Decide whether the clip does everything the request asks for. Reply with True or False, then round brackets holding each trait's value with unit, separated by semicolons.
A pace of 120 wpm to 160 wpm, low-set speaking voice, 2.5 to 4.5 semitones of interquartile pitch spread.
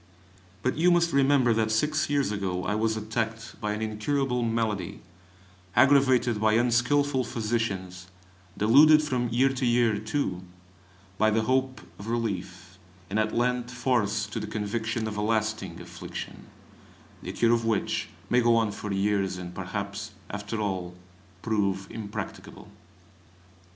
True (140 wpm; 110 Hz; 3.1 semitones)